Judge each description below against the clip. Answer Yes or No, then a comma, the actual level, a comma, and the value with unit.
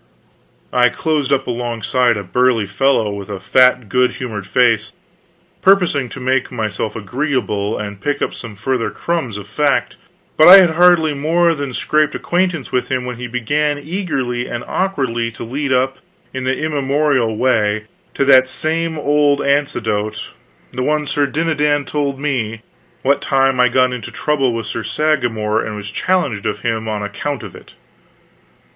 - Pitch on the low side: Yes, low, 130 Hz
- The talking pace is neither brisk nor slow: Yes, average, 165 wpm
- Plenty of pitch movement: No, average, 4.4 semitones